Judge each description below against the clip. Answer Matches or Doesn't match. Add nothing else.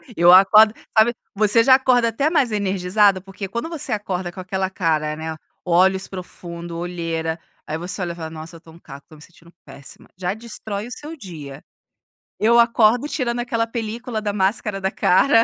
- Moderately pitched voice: Doesn't match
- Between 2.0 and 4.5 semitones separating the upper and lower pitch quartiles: Doesn't match